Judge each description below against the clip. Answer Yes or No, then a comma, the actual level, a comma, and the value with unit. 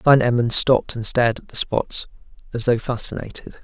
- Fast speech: No, average, 180 wpm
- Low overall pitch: Yes, low, 120 Hz